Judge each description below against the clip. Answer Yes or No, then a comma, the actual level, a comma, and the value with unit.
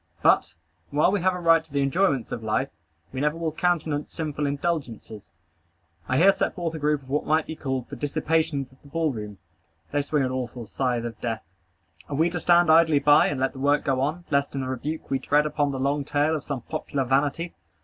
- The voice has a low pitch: No, medium, 145 Hz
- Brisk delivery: Yes, fast, 225 wpm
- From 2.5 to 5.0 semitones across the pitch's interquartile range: Yes, average, 3.2 semitones